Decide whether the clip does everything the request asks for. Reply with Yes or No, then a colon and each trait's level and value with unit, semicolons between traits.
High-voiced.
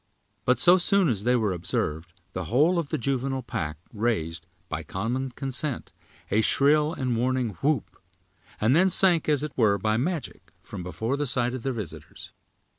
No: low, 125 Hz